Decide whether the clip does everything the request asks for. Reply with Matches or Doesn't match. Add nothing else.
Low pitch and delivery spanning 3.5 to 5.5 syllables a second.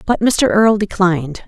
Doesn't match